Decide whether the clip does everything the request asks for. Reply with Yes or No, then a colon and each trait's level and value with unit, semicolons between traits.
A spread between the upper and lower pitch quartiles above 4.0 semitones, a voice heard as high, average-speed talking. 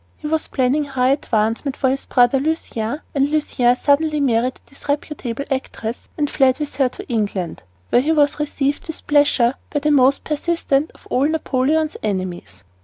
No: average, 3.3 semitones; very high, 275 Hz; average, 170 wpm